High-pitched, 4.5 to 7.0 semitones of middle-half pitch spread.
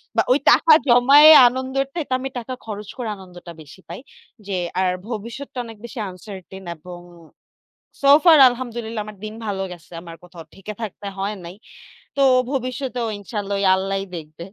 Yes: high, 215 Hz; average, 4.8 semitones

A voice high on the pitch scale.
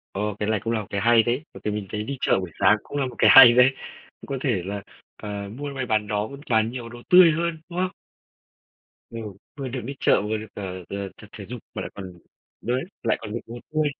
No: low, 115 Hz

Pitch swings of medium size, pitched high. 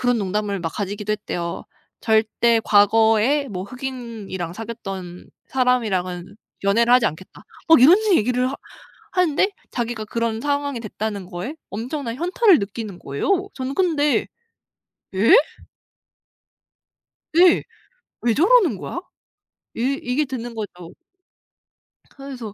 Yes: average, 5.0 semitones; high, 230 Hz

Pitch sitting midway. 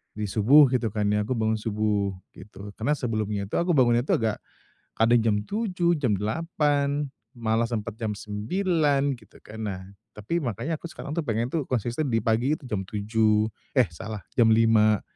No: low, 115 Hz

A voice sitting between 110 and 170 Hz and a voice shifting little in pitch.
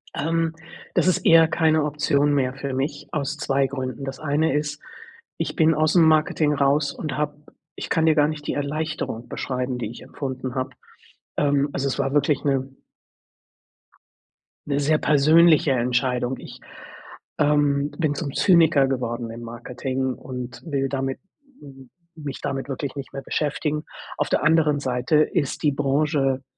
Yes: medium, 140 Hz; narrow, 2.3 semitones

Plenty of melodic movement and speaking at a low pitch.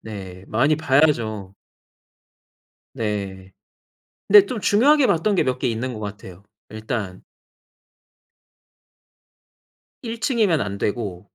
Yes: wide, 8.6 semitones; low, 115 Hz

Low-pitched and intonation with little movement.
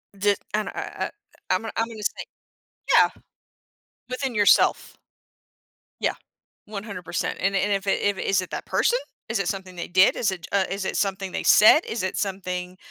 No: high, 195 Hz; narrow, 2.0 semitones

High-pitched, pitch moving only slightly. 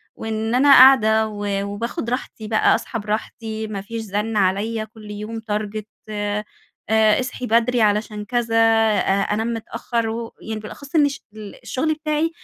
Yes: high, 220 Hz; narrow, 1.8 semitones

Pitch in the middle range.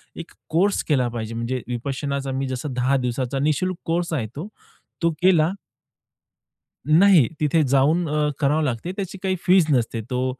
Yes: medium, 145 Hz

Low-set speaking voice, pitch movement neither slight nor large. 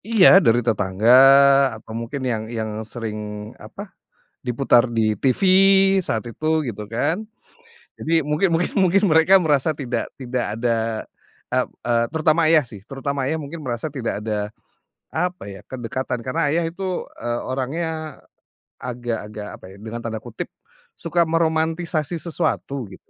No: low, 130 Hz; wide, 5.9 semitones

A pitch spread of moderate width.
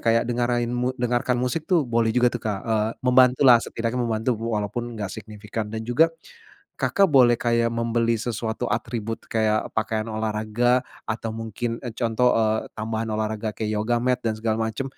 No: narrow, 1.7 semitones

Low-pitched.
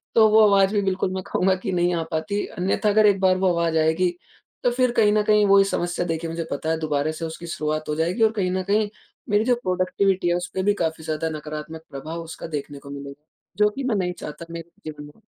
No: medium, 180 Hz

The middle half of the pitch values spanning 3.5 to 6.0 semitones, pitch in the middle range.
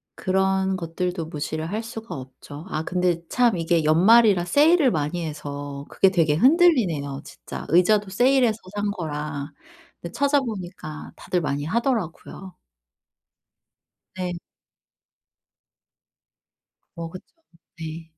Yes: wide, 5.5 semitones; medium, 180 Hz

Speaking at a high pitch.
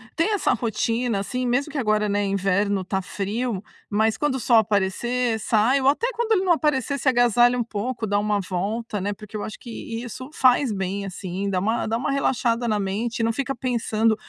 Yes: high, 225 Hz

